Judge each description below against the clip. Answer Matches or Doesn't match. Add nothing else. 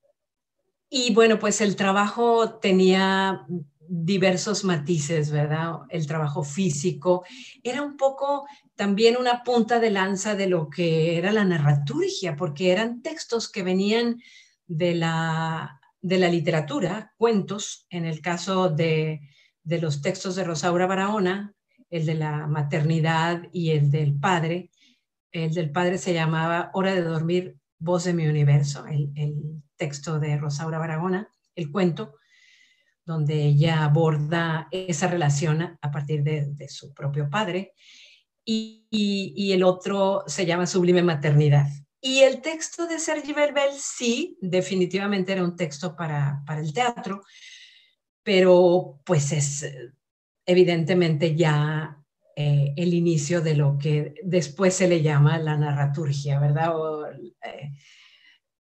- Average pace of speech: Matches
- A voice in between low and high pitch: Matches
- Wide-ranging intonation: Doesn't match